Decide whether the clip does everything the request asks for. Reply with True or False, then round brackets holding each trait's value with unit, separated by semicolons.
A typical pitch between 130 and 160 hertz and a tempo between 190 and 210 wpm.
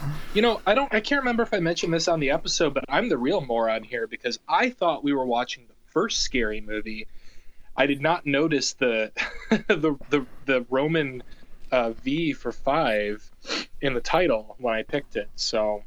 True (135 Hz; 195 wpm)